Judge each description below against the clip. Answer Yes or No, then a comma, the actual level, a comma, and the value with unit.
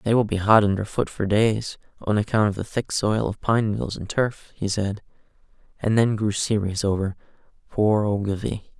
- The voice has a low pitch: Yes, low, 105 Hz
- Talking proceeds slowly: No, average, 190 wpm